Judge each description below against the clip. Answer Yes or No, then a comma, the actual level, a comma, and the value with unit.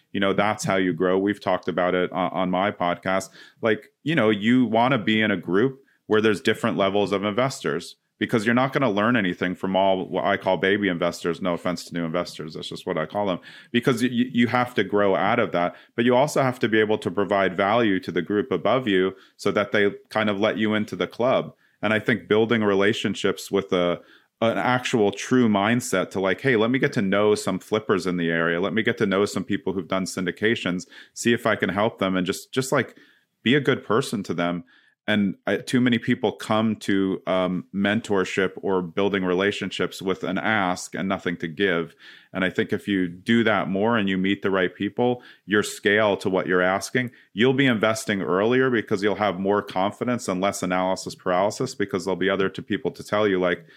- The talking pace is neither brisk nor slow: No, fast, 225 wpm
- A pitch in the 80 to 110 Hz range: Yes, low, 100 Hz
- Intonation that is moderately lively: Yes, average, 3.0 semitones